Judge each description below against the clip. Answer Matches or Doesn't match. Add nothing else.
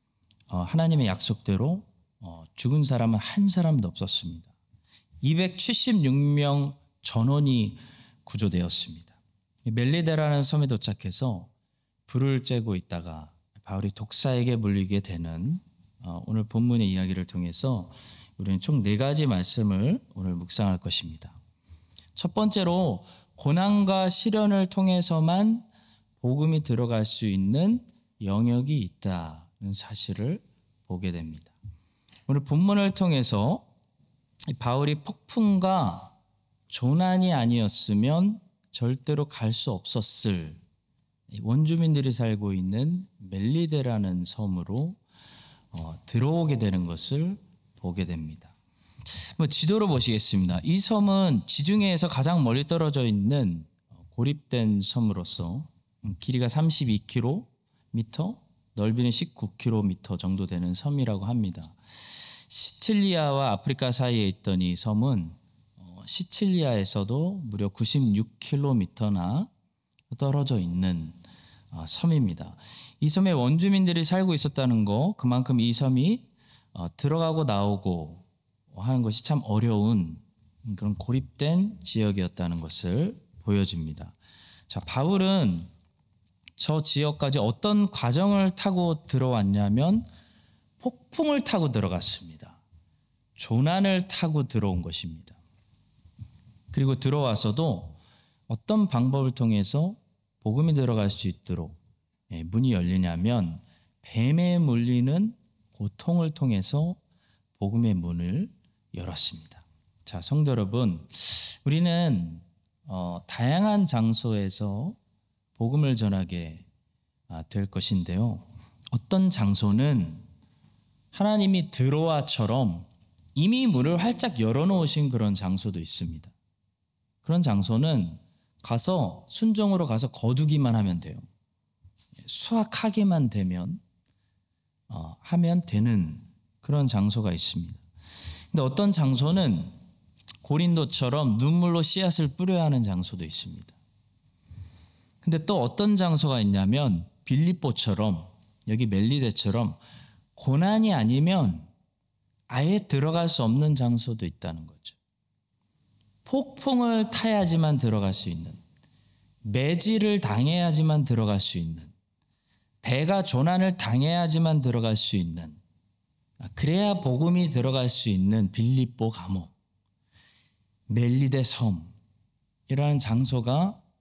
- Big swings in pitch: Matches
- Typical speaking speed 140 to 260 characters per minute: Matches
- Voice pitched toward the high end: Doesn't match